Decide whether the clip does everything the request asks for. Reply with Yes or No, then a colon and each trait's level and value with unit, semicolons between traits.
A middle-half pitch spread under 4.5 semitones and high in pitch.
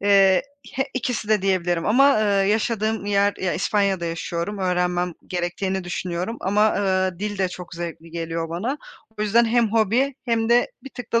Yes: average, 3.6 semitones; high, 200 Hz